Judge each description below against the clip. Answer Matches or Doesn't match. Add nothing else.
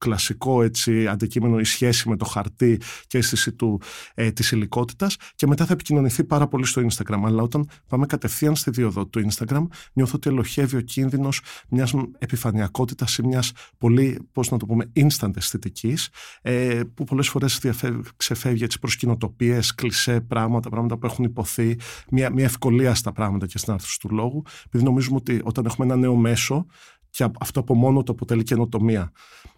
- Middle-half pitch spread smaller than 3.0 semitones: Matches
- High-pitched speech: Doesn't match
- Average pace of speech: Doesn't match